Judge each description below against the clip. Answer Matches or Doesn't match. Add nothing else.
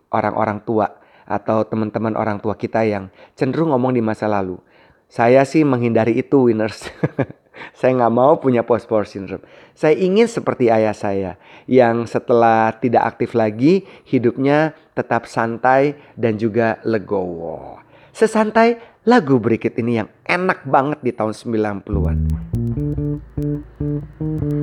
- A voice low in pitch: Matches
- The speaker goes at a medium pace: Matches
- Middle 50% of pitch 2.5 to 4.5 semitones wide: Doesn't match